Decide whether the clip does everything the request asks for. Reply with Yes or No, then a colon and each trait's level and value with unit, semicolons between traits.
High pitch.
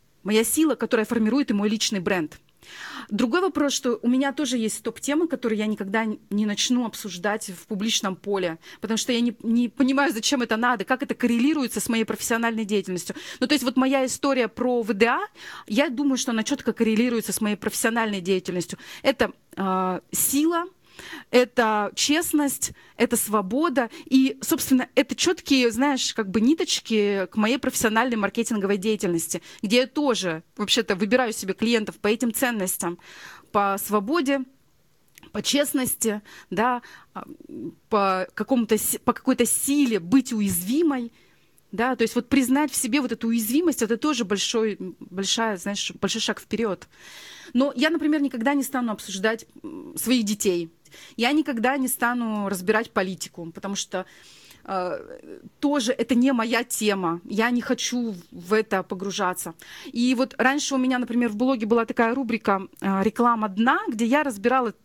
Yes: high, 230 Hz